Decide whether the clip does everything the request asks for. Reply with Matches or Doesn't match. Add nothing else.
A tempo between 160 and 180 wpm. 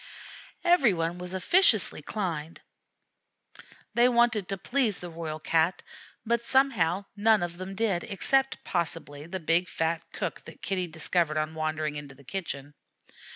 Doesn't match